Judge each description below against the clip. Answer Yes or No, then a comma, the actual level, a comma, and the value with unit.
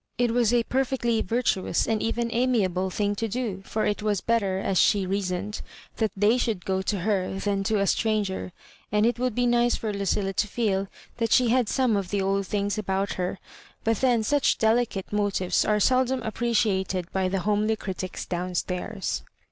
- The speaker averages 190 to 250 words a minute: Yes, average, 195 wpm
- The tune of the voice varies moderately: Yes, average, 3.2 semitones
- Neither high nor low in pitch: No, high, 210 Hz